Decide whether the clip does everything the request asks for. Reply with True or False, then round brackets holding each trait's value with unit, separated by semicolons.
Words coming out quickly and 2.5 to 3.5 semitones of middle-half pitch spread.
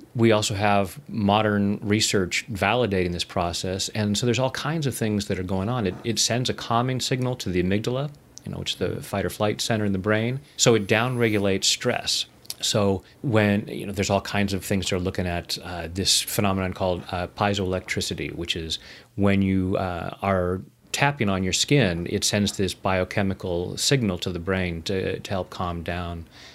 False (195 wpm; 3.0 semitones)